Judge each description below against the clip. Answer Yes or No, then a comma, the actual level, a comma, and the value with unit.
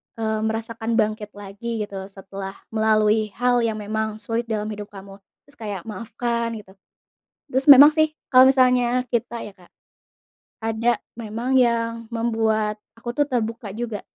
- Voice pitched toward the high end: Yes, high, 225 Hz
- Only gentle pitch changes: Yes, narrow, 2.0 semitones